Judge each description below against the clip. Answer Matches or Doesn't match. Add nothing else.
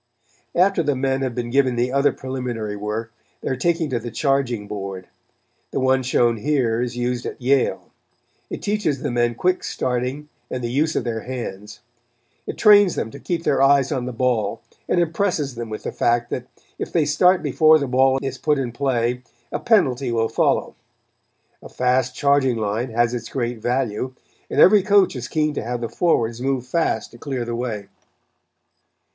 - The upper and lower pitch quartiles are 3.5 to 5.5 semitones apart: Doesn't match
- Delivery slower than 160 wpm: Doesn't match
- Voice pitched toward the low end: Matches